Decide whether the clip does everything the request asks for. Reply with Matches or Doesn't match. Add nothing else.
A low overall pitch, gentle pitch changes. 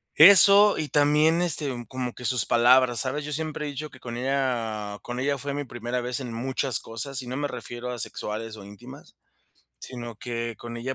Doesn't match